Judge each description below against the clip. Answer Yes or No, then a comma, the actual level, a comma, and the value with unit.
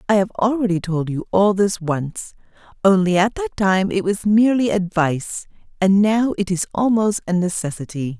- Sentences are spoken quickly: No, average, 170 wpm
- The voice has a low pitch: No, high, 190 Hz